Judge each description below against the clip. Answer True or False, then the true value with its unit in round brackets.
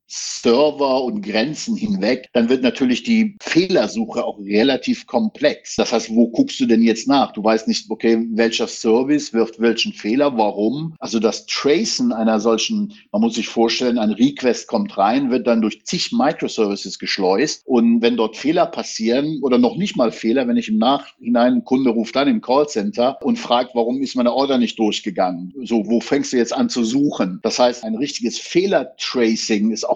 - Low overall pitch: True (125 Hz)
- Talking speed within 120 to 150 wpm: False (185 wpm)